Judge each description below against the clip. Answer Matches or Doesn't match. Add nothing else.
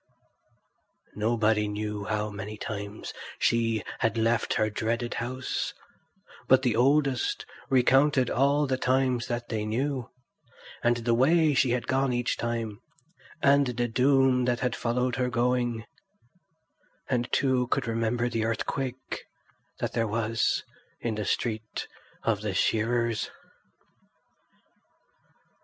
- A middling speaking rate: Doesn't match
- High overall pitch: Doesn't match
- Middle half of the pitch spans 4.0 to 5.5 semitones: Doesn't match